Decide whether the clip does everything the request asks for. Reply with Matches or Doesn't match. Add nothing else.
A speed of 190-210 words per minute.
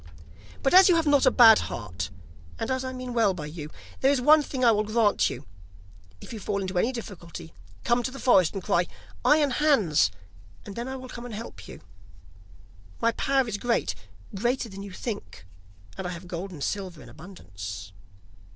Matches